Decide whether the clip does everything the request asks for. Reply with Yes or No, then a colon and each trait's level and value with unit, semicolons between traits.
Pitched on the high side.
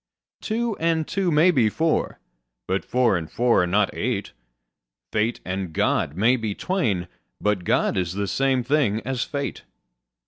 No: low, 120 Hz